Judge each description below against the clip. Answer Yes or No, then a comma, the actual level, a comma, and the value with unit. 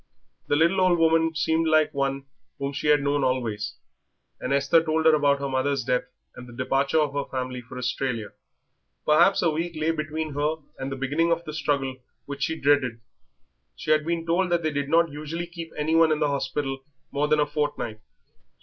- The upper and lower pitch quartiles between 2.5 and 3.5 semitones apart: Yes, average, 2.9 semitones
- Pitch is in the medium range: Yes, medium, 145 Hz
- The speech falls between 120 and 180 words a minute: No, average, 195 wpm